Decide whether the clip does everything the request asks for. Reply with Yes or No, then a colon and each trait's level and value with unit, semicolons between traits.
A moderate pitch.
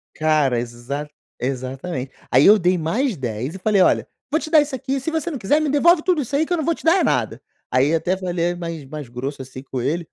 Yes: medium, 175 Hz